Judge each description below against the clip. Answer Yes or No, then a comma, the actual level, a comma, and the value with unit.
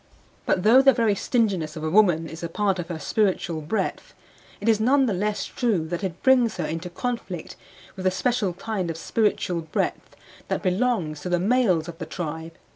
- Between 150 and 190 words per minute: No, average, 200 wpm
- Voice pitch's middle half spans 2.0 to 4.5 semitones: No, average, 5.1 semitones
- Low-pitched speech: No, medium, 185 Hz